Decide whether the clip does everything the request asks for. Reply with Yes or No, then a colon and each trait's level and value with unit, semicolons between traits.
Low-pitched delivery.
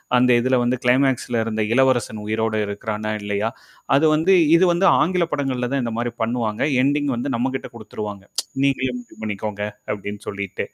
Yes: low, 120 Hz